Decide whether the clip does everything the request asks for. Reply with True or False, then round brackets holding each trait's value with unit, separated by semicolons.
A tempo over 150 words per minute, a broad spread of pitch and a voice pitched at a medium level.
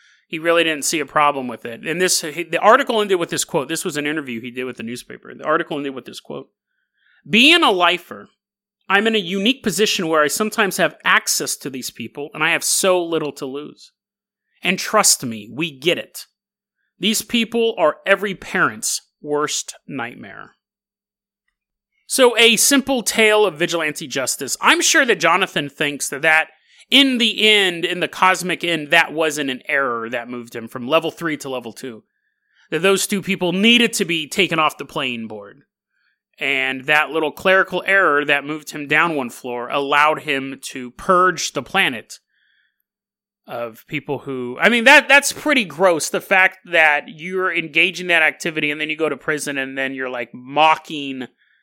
True (180 wpm; 5.9 semitones; 165 Hz)